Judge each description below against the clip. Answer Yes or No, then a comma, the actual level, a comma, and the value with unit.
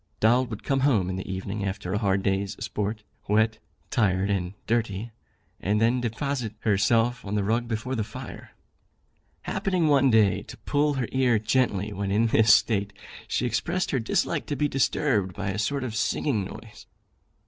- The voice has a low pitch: Yes, low, 110 Hz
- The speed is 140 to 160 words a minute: No, average, 175 wpm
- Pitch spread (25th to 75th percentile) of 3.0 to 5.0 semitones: Yes, average, 3.8 semitones